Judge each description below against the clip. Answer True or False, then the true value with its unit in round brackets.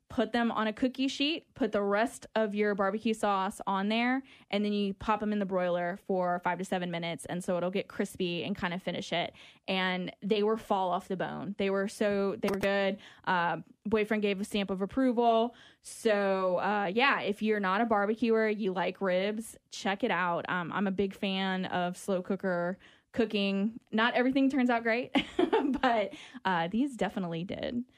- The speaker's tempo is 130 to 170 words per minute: False (195 wpm)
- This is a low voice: False (205 Hz)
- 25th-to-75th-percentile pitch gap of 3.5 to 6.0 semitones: False (3.1 semitones)